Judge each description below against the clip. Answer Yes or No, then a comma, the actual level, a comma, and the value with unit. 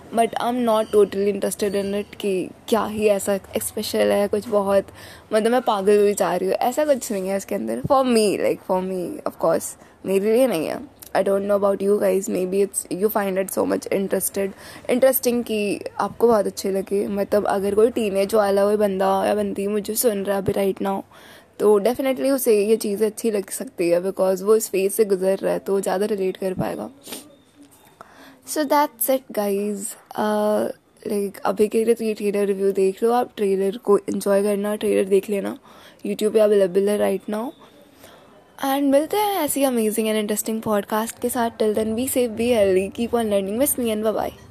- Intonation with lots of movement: No, narrow, 2.5 semitones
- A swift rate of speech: Yes, fast, 210 wpm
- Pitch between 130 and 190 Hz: No, high, 210 Hz